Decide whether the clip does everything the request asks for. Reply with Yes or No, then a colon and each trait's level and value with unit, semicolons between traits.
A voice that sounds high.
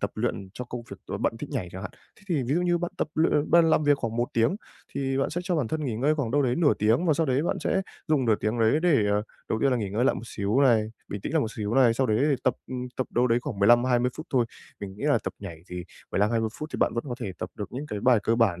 No: low, 125 Hz